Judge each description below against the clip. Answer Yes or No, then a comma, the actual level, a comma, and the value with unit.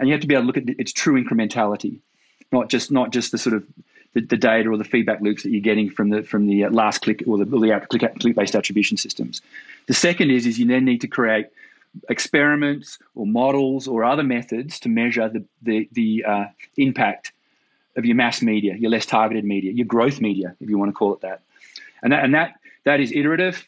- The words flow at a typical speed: No, fast, 230 wpm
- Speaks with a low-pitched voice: Yes, low, 120 Hz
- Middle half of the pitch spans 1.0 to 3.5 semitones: No, average, 4.3 semitones